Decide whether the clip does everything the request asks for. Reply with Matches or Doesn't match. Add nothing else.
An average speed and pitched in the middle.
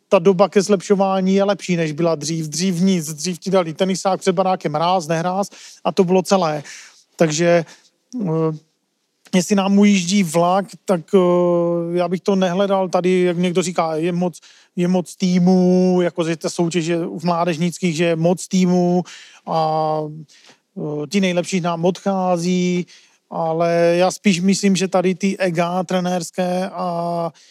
Matches